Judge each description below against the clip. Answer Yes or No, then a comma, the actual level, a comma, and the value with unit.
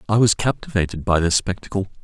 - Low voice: Yes, very low, 95 Hz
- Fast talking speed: No, average, 175 wpm